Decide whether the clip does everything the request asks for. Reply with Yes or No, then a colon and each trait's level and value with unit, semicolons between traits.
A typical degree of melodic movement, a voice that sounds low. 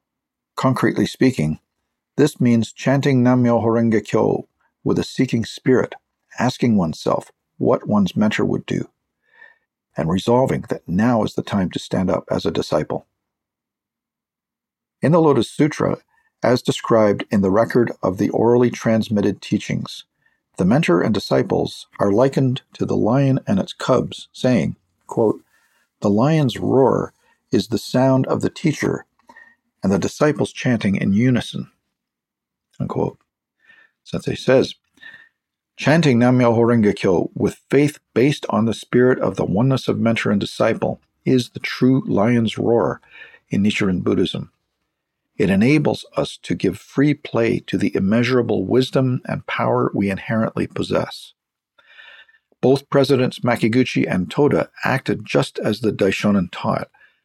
Yes: average, 3.6 semitones; low, 125 Hz